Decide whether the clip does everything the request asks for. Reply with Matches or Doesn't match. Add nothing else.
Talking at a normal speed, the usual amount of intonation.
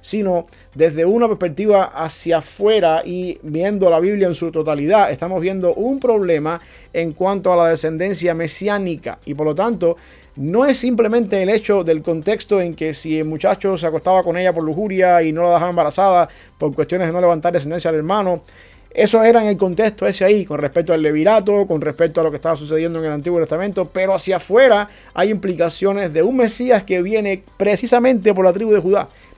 Matches